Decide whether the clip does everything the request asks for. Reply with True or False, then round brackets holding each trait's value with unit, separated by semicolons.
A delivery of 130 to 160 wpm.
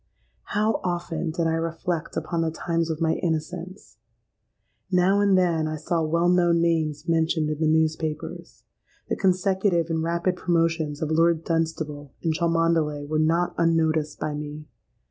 True (150 wpm)